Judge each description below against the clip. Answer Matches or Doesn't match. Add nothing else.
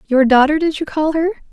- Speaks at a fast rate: Matches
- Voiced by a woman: Matches